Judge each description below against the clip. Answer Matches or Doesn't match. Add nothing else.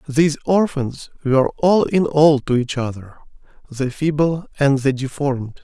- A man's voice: Matches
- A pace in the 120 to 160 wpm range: Matches